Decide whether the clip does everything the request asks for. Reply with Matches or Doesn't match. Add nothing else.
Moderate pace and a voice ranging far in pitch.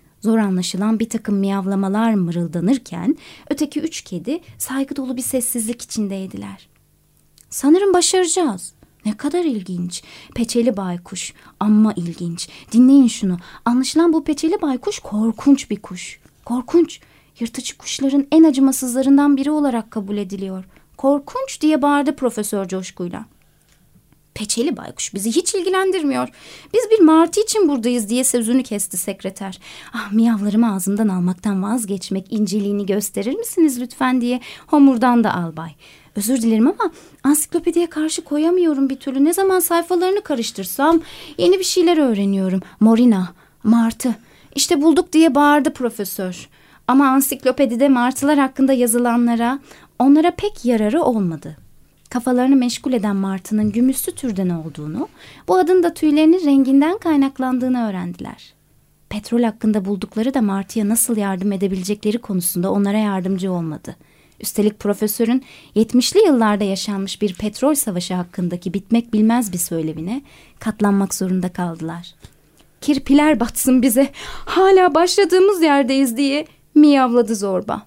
Matches